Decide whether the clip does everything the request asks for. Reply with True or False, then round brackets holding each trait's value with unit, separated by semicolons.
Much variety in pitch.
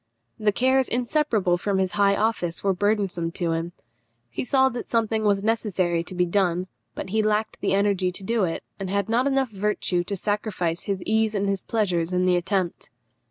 False (3.2 semitones)